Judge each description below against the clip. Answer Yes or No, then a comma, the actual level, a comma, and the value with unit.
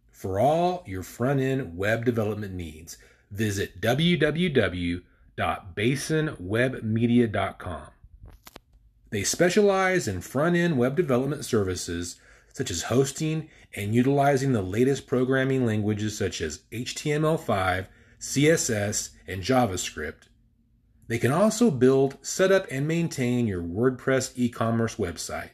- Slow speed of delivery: Yes, slow, 110 wpm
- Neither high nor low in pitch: No, low, 120 Hz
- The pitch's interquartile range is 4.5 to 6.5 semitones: Yes, average, 4.9 semitones